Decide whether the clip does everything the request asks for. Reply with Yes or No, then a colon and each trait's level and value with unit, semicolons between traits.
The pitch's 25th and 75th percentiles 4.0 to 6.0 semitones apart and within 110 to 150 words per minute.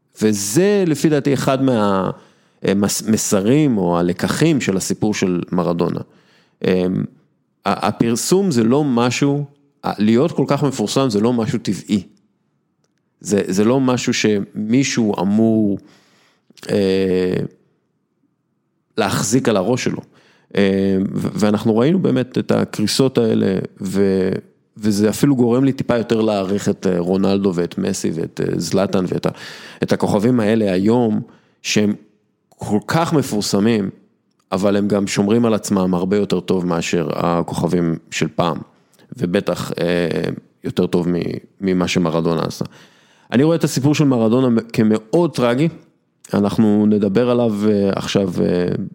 Yes: average, 4.4 semitones; average, 120 wpm